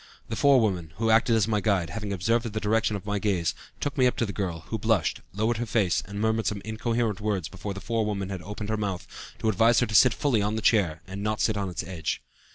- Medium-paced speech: No, fast, 245 wpm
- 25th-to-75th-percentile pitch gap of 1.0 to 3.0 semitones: Yes, narrow, 2.4 semitones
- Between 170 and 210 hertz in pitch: No, low, 105 Hz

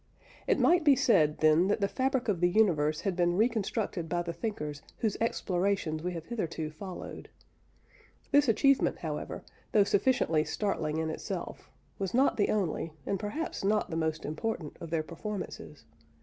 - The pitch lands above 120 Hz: Yes, medium, 185 Hz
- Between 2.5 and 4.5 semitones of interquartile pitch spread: No, average, 5.2 semitones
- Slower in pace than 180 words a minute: Yes, average, 165 wpm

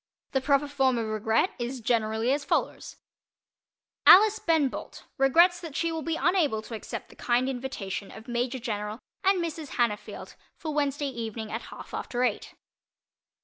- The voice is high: Yes, very high, 260 Hz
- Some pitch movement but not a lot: Yes, average, 5.0 semitones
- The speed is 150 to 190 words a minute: Yes, average, 160 wpm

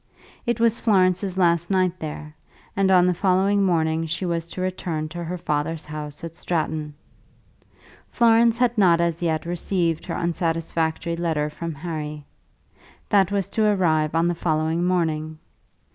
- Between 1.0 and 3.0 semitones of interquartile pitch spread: Yes, average, 2.7 semitones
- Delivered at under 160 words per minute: Yes, average, 150 wpm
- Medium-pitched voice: Yes, medium, 170 Hz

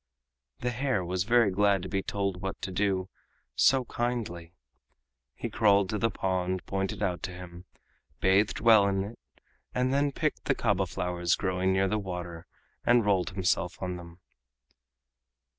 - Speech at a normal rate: Yes, average, 160 wpm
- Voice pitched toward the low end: Yes, very low, 95 Hz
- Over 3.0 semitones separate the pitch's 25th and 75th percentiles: No, average, 2.7 semitones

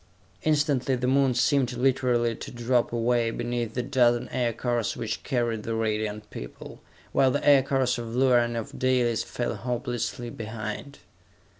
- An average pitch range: No, narrow, 1.9 semitones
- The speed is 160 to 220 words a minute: No, average, 145 wpm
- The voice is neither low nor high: No, low, 120 Hz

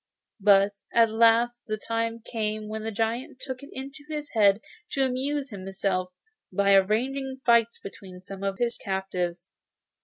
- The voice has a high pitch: Yes, high, 220 Hz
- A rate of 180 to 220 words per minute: No, average, 150 wpm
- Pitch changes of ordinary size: Yes, average, 3.9 semitones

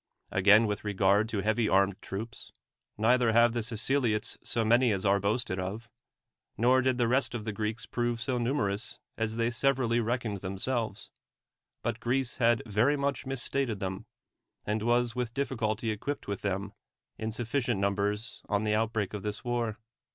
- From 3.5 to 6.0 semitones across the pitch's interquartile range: No, average, 2.8 semitones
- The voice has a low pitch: Yes, low, 110 Hz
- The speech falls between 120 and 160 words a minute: No, average, 170 wpm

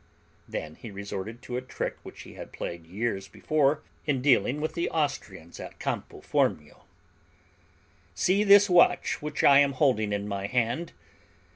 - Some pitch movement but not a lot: No, wide, 7.1 semitones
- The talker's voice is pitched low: Yes, low, 125 Hz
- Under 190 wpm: Yes, average, 155 wpm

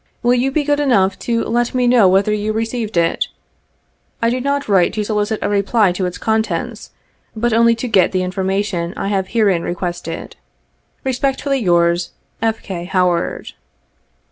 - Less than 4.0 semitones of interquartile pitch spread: No, average, 4.5 semitones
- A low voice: No, high, 210 Hz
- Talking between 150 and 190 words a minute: Yes, average, 170 wpm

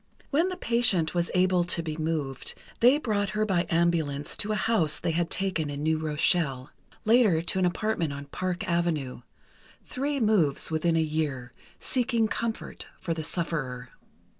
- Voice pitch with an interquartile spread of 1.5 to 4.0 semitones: No, wide, 5.4 semitones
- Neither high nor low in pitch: Yes, medium, 170 Hz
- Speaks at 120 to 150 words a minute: No, average, 160 wpm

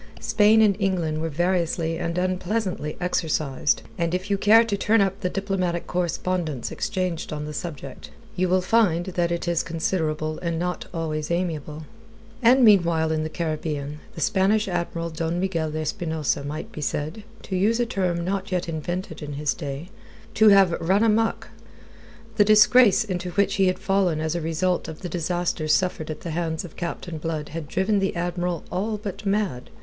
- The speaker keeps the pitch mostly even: No, average, 3.3 semitones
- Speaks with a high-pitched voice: No, medium, 175 Hz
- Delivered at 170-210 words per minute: Yes, average, 180 wpm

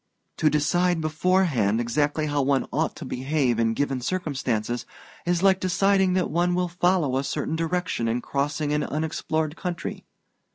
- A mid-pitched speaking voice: Yes, medium, 155 Hz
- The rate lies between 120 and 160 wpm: Yes, average, 155 wpm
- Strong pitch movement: No, average, 4.5 semitones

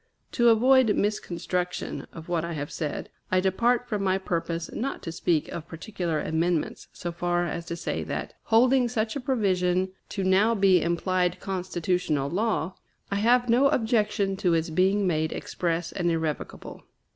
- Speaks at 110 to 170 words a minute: Yes, average, 160 wpm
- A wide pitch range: No, average, 4.3 semitones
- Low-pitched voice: No, medium, 185 Hz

